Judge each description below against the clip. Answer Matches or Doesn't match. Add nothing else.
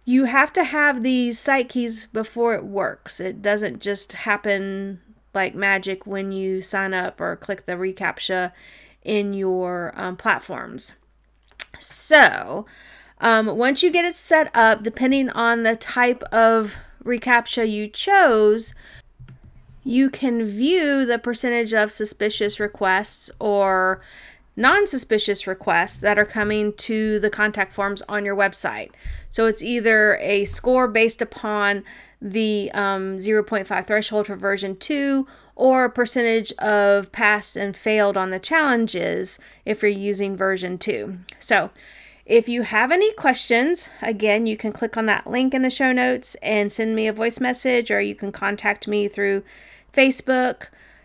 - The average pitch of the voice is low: Doesn't match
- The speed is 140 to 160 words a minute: Matches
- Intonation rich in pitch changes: Doesn't match